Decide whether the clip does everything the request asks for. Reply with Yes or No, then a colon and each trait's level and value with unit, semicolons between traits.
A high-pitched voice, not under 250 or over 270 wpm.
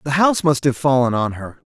No: medium, 140 Hz; fast, 255 wpm